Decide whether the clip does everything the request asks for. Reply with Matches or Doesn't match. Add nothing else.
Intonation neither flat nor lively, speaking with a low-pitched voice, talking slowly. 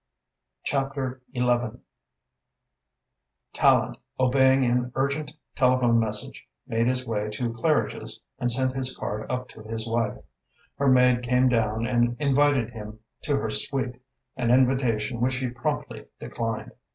Doesn't match